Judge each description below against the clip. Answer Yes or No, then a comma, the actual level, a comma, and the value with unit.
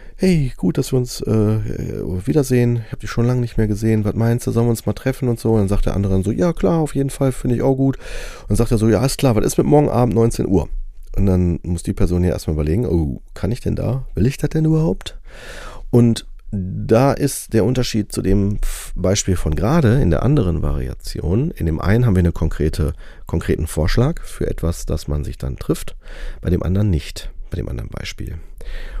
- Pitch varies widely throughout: Yes, wide, 5.8 semitones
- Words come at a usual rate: No, fast, 230 wpm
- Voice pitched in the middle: No, low, 105 Hz